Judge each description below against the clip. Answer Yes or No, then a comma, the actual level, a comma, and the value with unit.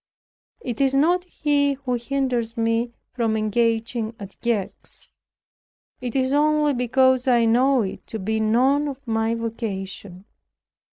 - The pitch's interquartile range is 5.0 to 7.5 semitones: No, average, 3.4 semitones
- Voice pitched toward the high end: Yes, high, 240 Hz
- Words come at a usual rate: No, slow, 130 wpm